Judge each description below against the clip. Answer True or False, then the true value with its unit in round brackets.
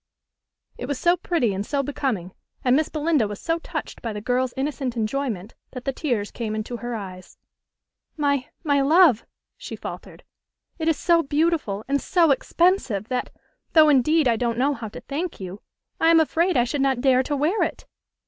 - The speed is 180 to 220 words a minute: True (185 wpm)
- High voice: True (270 Hz)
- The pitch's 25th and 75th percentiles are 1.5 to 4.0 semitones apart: False (5.1 semitones)